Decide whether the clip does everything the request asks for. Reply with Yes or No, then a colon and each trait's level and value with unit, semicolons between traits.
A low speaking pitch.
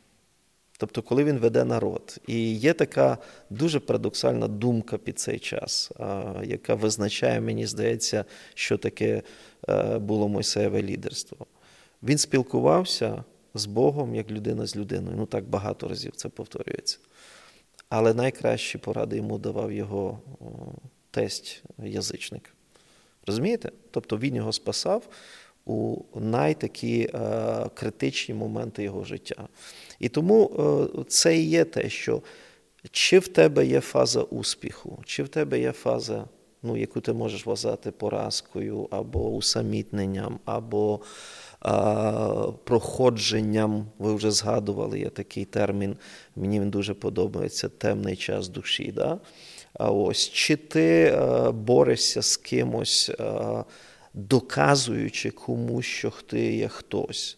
Yes: low, 110 Hz